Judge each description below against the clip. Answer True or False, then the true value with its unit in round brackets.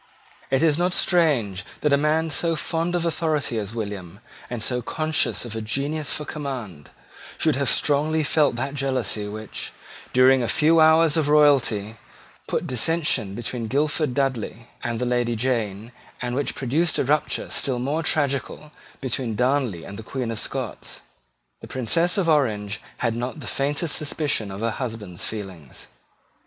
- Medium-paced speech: True (160 wpm)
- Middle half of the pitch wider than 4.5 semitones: True (5.2 semitones)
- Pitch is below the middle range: True (130 Hz)